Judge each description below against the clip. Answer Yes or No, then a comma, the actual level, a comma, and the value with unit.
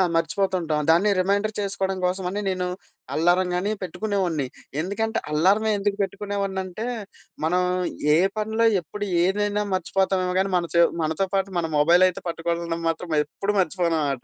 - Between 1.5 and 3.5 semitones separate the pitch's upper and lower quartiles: Yes, average, 2.9 semitones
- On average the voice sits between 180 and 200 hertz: Yes, medium, 185 Hz